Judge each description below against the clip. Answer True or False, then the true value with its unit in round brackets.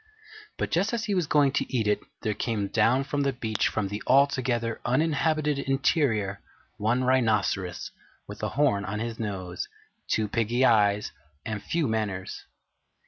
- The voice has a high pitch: False (115 Hz)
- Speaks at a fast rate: False (155 wpm)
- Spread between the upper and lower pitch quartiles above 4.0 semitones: True (4.9 semitones)